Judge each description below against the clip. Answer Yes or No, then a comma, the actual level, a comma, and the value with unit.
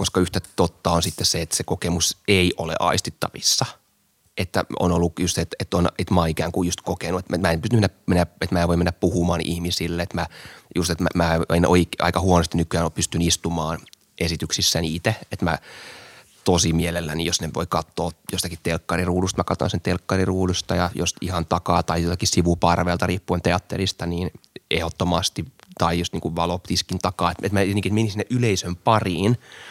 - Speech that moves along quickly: Yes, fast, 185 wpm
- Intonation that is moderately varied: No, narrow, 1.7 semitones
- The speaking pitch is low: Yes, very low, 90 Hz